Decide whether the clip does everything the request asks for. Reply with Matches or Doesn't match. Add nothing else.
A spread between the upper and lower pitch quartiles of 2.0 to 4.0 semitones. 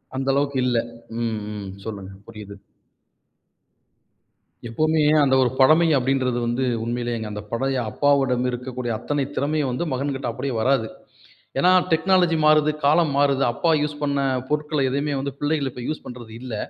Matches